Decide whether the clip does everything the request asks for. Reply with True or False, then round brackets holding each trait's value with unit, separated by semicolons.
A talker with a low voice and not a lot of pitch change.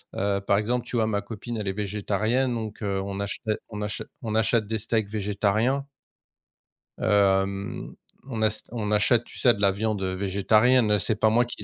True (105 Hz; 2.0 semitones)